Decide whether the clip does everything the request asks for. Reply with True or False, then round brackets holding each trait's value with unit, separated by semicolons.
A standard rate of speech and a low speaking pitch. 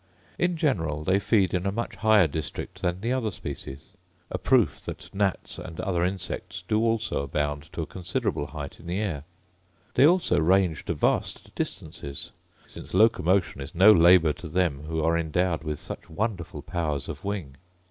True (175 wpm; 90 Hz)